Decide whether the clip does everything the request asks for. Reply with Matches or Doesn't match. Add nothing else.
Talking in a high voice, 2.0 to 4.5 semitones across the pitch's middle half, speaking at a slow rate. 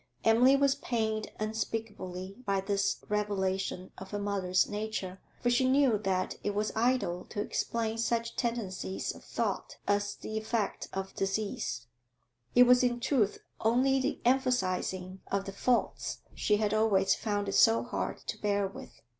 Doesn't match